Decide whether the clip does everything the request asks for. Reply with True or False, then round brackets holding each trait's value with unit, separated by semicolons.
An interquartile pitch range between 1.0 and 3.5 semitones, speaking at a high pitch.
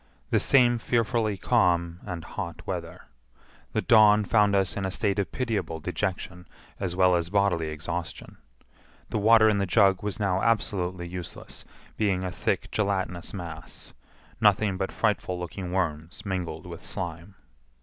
False (2.9 semitones; 95 Hz)